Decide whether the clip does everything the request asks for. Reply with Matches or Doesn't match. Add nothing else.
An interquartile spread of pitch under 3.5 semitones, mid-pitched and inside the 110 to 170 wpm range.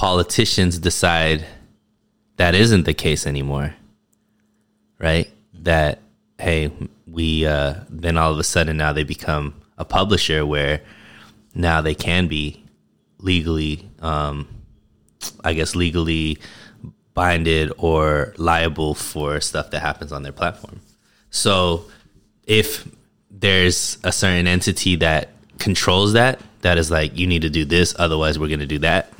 Doesn't match